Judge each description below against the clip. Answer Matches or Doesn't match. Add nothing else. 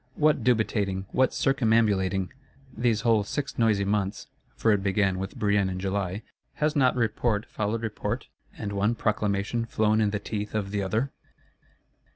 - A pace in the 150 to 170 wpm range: Matches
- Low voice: Matches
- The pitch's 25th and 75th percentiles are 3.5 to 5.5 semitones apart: Doesn't match